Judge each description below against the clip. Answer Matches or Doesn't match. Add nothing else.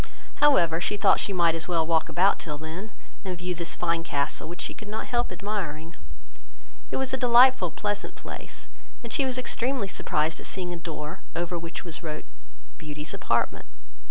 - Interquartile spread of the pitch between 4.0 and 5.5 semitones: Matches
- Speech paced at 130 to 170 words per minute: Doesn't match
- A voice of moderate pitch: Matches